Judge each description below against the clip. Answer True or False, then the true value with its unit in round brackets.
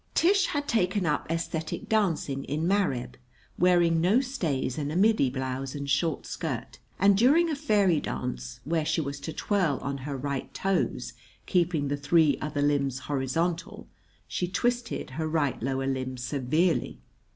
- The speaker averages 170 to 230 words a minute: False (155 wpm)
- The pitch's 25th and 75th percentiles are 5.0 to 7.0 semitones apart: True (5.3 semitones)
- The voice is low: False (160 Hz)